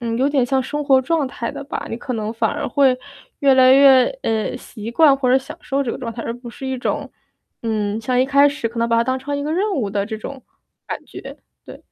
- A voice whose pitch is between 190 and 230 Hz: No, very high, 255 Hz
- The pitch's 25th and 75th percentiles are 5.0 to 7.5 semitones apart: No, average, 3.2 semitones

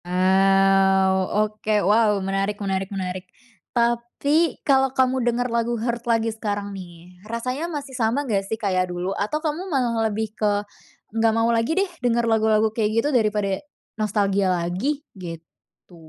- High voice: Yes, high, 215 Hz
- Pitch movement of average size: Yes, average, 3.5 semitones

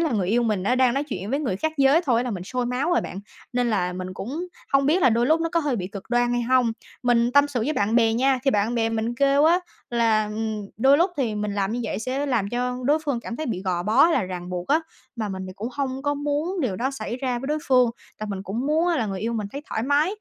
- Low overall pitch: No, high, 245 Hz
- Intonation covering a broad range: No, average, 4.7 semitones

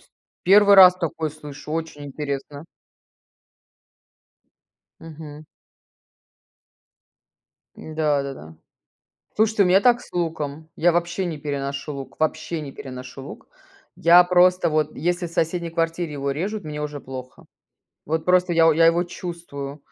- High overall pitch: No, medium, 160 Hz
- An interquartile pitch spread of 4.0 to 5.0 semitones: No, average, 3.3 semitones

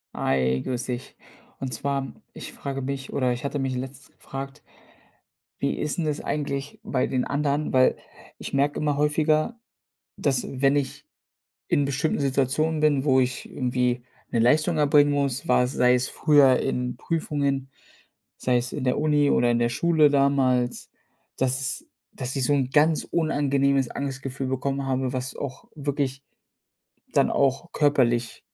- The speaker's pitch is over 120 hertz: Yes, low, 135 Hz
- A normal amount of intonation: No, narrow, 2.2 semitones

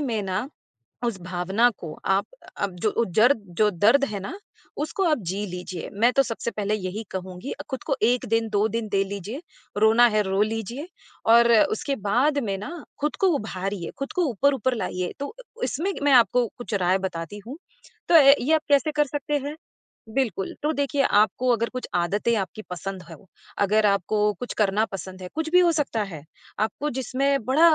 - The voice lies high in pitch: Yes, high, 225 Hz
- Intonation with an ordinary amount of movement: No, wide, 5.9 semitones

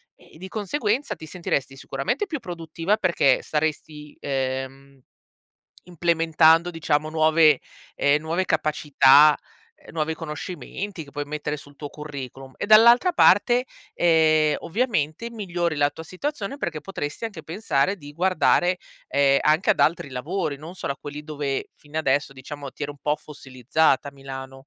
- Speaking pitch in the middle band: Yes, medium, 155 Hz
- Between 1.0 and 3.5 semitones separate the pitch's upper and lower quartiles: No, average, 3.9 semitones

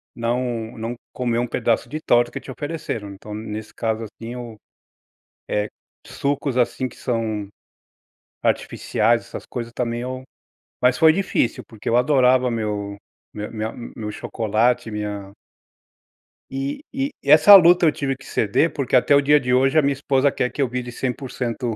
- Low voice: Yes, low, 120 Hz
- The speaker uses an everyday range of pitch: Yes, average, 3.3 semitones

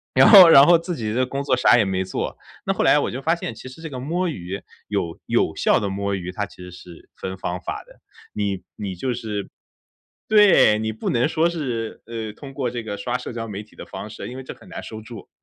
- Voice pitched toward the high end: No, low, 115 Hz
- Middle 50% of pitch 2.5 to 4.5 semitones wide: No, wide, 5.4 semitones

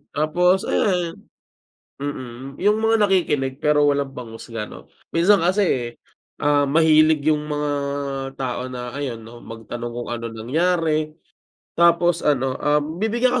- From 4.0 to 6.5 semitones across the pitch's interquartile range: Yes, average, 5.2 semitones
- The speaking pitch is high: No, medium, 150 Hz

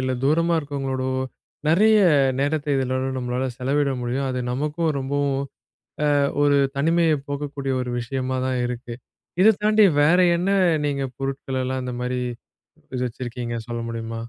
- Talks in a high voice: No, low, 135 Hz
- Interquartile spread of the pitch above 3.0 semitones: No, narrow, 2.5 semitones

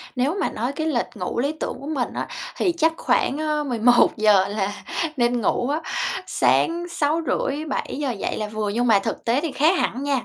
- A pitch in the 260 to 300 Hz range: Yes, very high, 265 Hz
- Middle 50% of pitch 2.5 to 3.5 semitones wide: No, average, 5.1 semitones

